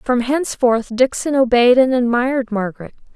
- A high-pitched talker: Yes, high, 245 Hz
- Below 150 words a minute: Yes, slow, 135 wpm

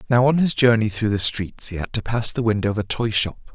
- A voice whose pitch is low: Yes, low, 110 Hz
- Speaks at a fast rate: Yes, fast, 290 wpm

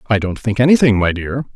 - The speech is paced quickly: Yes, fast, 230 wpm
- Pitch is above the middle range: No, low, 115 Hz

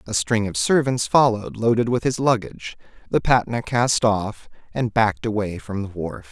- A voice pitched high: No, low, 110 Hz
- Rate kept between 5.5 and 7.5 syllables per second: No, 5.0 syllables/s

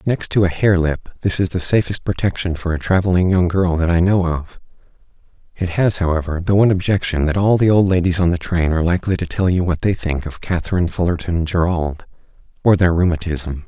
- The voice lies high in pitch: No, very low, 90 Hz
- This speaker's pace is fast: Yes, fast, 210 wpm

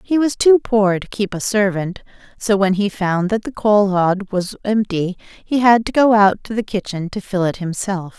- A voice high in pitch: Yes, high, 200 Hz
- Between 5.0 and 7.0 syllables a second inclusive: No, 4.6 syllables/s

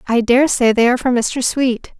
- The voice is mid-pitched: No, high, 245 Hz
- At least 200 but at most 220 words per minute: No, fast, 240 wpm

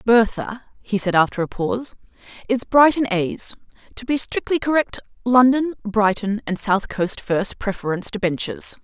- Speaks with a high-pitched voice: Yes, high, 220 Hz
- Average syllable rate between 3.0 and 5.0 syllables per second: Yes, 4.9 syllables/s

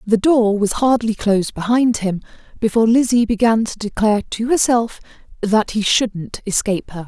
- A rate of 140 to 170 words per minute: Yes, average, 160 wpm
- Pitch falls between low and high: No, high, 220 Hz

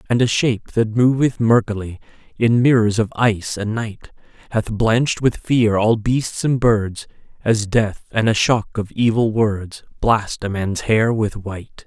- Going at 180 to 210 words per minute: No, average, 170 wpm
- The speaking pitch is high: No, low, 110 Hz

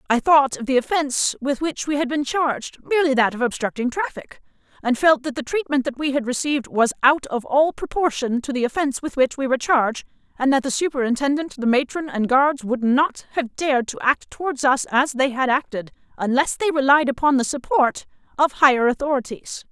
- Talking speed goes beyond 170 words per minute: Yes, average, 200 wpm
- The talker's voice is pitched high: Yes, very high, 270 Hz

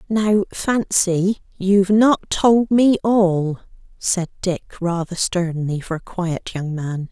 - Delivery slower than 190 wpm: Yes, slow, 135 wpm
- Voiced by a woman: Yes, female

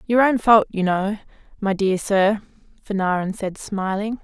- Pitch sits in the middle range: No, high, 205 Hz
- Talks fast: No, average, 155 wpm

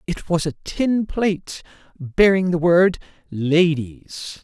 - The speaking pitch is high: No, medium, 170 Hz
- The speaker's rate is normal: No, slow, 120 wpm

